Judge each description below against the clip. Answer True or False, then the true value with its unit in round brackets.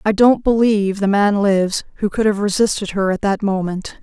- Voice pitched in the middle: False (205 Hz)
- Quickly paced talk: True (210 wpm)